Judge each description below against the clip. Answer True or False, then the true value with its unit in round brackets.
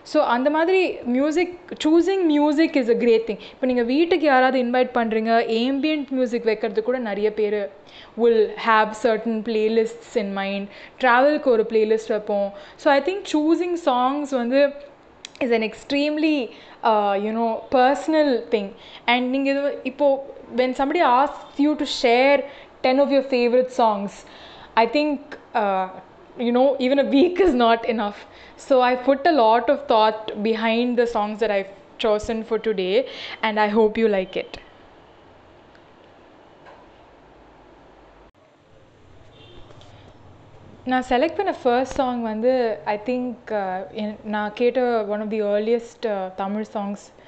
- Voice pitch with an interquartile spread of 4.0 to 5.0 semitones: True (4.3 semitones)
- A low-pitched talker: False (235 Hz)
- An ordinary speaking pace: False (140 wpm)